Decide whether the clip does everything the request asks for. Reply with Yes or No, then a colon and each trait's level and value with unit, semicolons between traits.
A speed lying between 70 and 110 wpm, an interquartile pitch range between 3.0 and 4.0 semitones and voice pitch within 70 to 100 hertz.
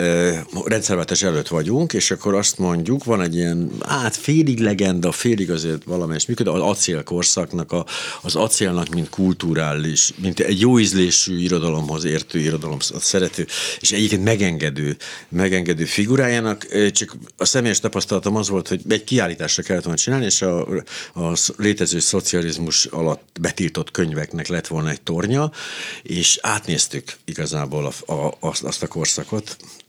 No: average, 145 wpm; average, 3.7 semitones; very low, 90 Hz